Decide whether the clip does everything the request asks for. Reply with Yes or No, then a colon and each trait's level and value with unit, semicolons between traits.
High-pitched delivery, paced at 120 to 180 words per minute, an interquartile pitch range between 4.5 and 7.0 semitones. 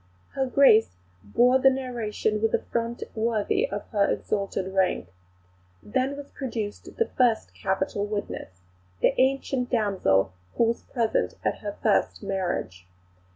Yes: high, 220 Hz; slow, 135 wpm; average, 4.8 semitones